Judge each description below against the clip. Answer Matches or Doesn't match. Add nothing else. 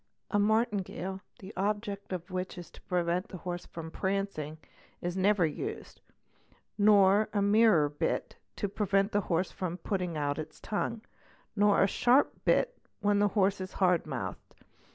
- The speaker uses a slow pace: Doesn't match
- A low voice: Doesn't match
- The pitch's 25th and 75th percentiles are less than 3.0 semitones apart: Matches